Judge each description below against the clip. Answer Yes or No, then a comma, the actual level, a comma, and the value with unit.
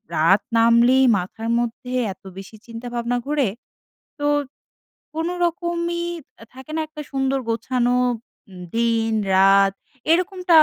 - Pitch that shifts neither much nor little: No, wide, 5.8 semitones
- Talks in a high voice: Yes, very high, 250 Hz